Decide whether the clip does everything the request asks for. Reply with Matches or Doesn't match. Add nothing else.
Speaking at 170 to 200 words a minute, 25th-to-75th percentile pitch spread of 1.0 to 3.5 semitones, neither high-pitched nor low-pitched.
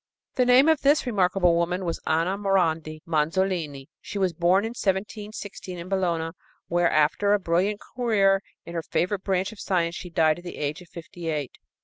Matches